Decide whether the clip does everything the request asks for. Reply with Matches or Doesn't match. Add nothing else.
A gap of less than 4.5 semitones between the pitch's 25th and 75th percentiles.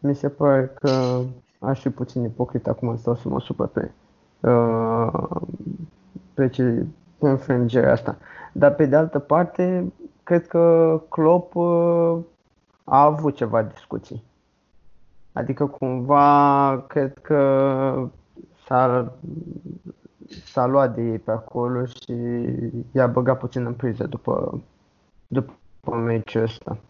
Matches